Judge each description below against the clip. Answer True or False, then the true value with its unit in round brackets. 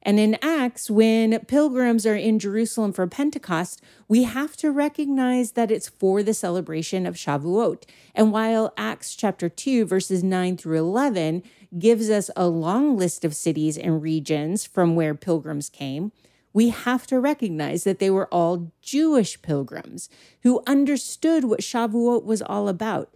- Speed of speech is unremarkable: True (155 wpm)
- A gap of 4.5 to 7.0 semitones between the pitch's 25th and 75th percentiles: True (5.6 semitones)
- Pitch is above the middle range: True (210 Hz)